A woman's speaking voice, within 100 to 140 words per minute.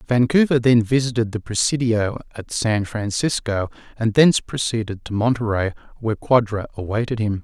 No: male; slow, 135 wpm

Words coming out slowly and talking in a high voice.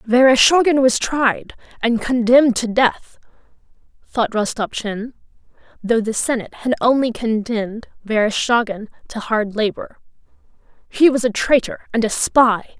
Yes: slow, 120 wpm; high, 235 Hz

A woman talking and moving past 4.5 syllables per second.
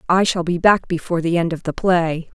Yes: female; 5.6 syllables/s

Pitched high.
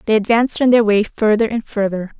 Yes: high, 220 Hz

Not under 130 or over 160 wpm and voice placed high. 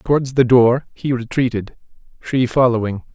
No: slow, 135 wpm; low, 125 Hz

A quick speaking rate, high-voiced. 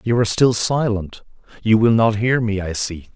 No: fast, 210 wpm; low, 110 Hz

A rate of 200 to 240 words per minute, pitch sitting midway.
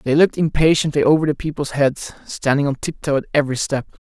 Yes: fast, 205 wpm; medium, 145 Hz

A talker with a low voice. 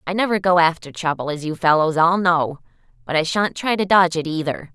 No: medium, 170 Hz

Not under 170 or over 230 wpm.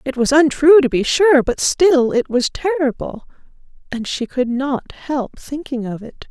Yes: average, 180 wpm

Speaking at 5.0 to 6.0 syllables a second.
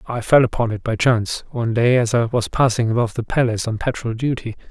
No: 6.4 syllables/s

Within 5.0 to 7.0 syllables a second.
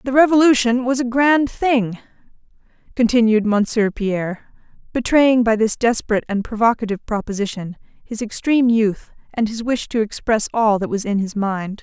Yes: 5.2 syllables/s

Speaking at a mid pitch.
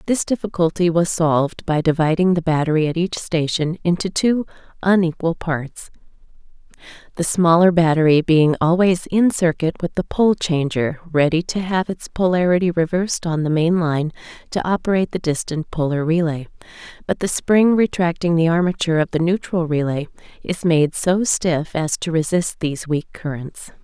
Yes: medium, 170 Hz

